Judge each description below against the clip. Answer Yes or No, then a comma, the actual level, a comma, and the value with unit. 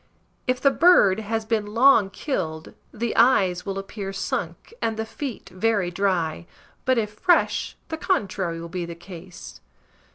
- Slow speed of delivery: No, average, 155 wpm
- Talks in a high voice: Yes, high, 200 Hz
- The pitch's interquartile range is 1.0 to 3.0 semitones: No, average, 4.2 semitones